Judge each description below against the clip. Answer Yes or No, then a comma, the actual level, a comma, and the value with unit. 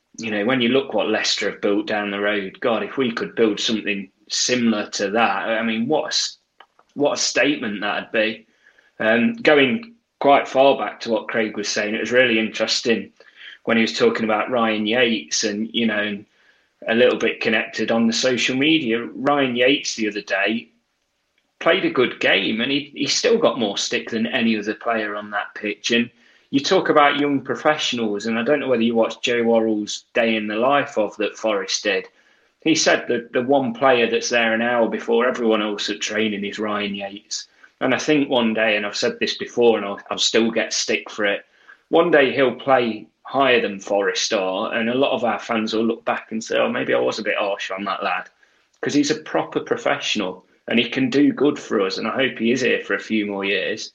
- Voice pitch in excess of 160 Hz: No, low, 115 Hz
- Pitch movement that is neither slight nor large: Yes, average, 3.5 semitones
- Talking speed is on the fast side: Yes, fast, 220 wpm